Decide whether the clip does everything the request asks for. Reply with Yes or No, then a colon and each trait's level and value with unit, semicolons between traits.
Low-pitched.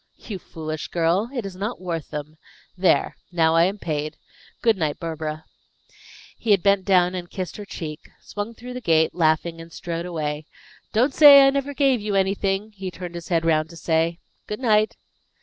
No: medium, 180 Hz